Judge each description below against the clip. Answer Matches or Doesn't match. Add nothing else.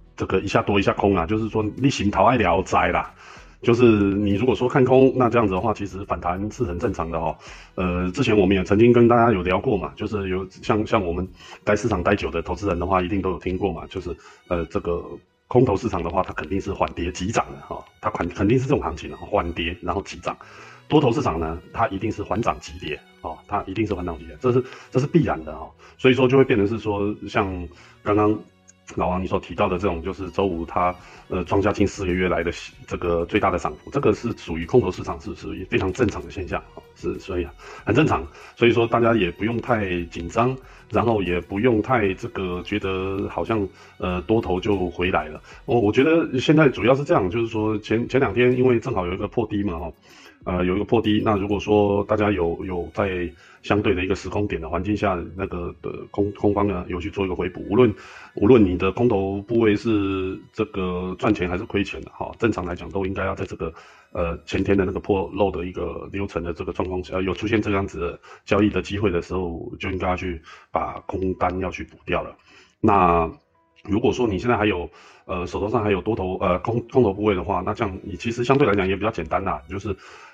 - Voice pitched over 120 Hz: Doesn't match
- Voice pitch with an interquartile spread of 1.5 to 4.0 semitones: Matches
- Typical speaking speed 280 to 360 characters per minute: Matches